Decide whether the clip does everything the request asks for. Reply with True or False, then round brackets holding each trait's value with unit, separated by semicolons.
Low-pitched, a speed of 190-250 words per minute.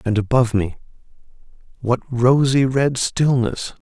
False (125 Hz; 95 wpm)